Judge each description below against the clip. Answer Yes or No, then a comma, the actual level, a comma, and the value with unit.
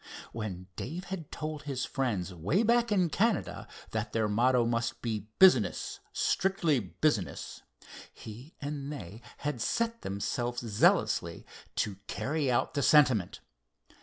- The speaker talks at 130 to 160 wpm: Yes, slow, 135 wpm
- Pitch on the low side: Yes, low, 130 Hz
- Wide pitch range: Yes, wide, 6.2 semitones